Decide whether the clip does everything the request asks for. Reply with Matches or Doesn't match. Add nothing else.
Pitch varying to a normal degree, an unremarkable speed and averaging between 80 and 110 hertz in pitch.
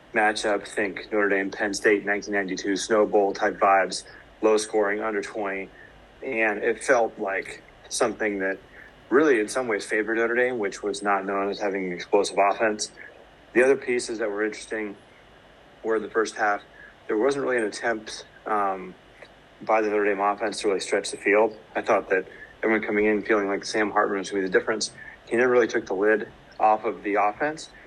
Doesn't match